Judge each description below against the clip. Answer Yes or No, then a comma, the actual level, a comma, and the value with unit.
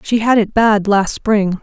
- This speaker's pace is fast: Yes, fast, 220 wpm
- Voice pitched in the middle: No, high, 210 Hz